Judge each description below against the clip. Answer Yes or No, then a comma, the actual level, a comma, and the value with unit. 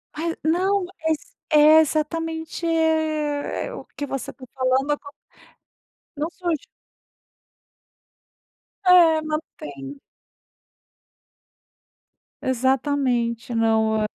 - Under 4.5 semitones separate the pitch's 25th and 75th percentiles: Yes, average, 3.9 semitones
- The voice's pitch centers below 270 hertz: No, very high, 300 Hz